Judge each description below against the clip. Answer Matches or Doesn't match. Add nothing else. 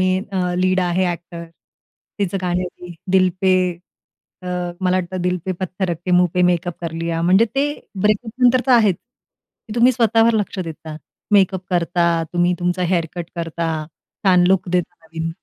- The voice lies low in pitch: Doesn't match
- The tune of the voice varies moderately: Doesn't match